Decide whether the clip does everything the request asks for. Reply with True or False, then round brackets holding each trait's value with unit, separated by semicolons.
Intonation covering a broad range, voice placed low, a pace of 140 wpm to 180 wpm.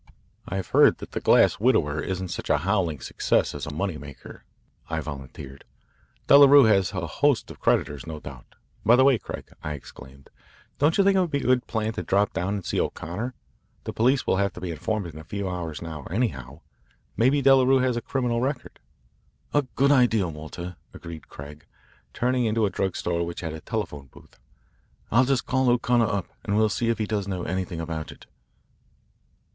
False (7.2 semitones; 100 Hz; 195 wpm)